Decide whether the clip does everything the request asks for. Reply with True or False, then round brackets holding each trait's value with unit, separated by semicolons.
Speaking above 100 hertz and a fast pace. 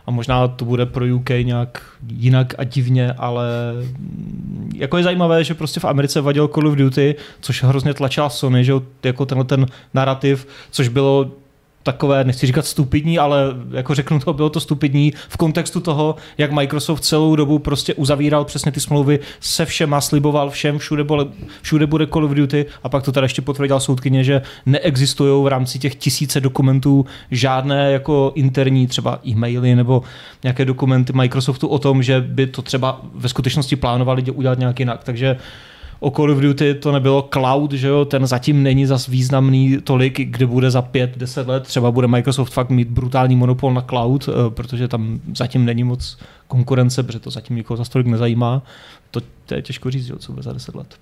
True (135 Hz; 185 wpm)